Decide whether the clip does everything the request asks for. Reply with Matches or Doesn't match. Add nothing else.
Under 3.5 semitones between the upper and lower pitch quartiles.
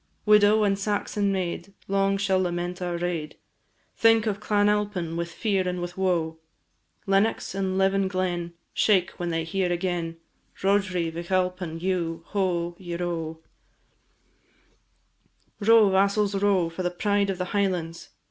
Matches